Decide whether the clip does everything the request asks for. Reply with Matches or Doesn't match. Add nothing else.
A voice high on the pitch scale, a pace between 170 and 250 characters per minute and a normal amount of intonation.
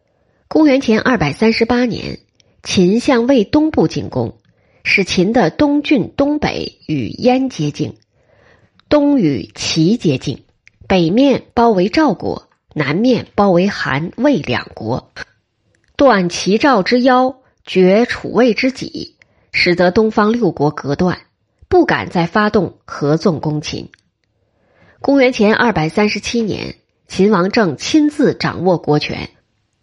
Doesn't match